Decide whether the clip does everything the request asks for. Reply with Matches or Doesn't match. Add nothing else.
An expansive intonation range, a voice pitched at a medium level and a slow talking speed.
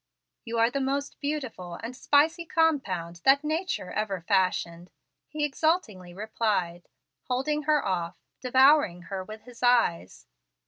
Doesn't match